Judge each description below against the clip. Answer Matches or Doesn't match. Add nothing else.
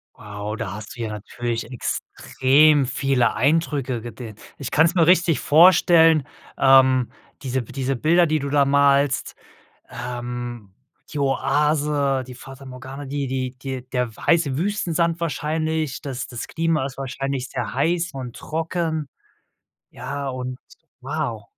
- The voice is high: Doesn't match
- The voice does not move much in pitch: Doesn't match